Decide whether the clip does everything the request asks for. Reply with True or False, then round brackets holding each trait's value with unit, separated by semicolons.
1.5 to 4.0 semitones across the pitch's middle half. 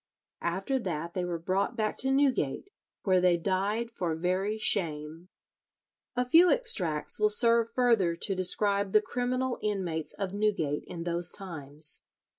False (5.3 semitones)